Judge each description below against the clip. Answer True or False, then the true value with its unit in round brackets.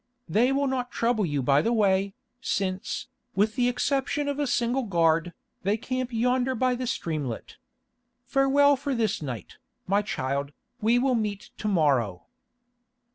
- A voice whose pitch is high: True (220 Hz)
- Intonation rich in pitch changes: True (6.8 semitones)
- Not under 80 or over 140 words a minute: False (150 wpm)